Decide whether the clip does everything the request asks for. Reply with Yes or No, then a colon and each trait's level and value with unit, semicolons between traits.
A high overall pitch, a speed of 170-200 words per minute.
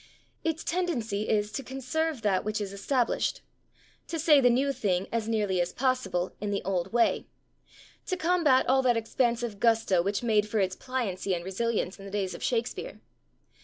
Yes: high, 225 Hz; average, 175 wpm